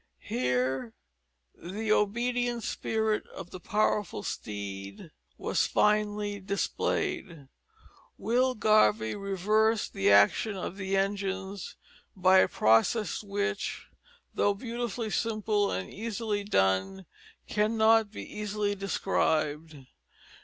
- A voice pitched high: Yes, high, 200 Hz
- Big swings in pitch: Yes, wide, 6.0 semitones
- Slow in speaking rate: Yes, slow, 95 wpm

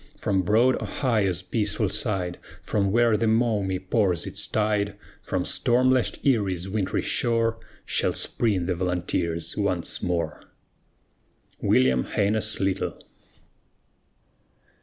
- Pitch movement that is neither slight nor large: Yes, average, 3.4 semitones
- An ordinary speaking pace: No, slow, 110 wpm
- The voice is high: No, low, 100 Hz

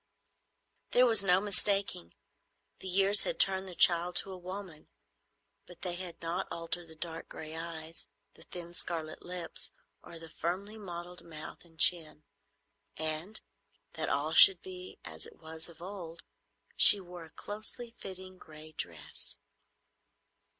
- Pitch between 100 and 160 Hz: No, medium, 175 Hz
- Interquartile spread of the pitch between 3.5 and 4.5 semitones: No, average, 3.0 semitones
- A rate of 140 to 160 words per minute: Yes, average, 145 wpm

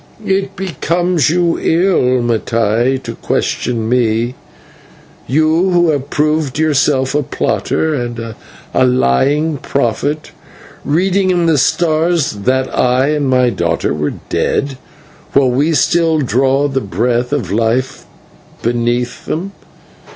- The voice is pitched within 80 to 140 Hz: Yes, low, 135 Hz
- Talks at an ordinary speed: No, slow, 120 wpm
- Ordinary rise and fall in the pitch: Yes, average, 4.7 semitones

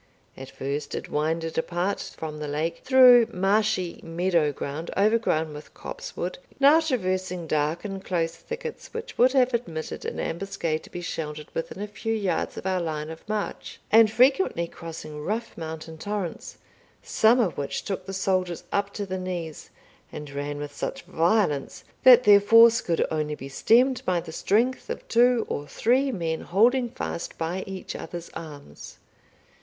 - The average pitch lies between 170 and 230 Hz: Yes, medium, 185 Hz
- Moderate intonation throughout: No, wide, 5.8 semitones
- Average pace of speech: Yes, average, 165 wpm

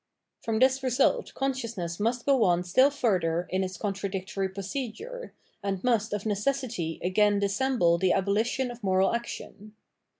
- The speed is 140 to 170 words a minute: Yes, average, 155 wpm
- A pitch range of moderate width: Yes, average, 4.8 semitones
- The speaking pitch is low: No, high, 210 Hz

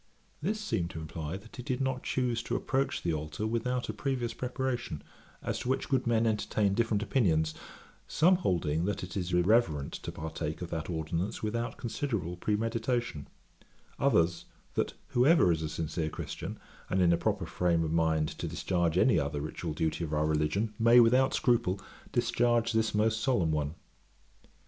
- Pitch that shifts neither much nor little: No, wide, 6.8 semitones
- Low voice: Yes, low, 100 Hz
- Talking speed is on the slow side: No, average, 170 wpm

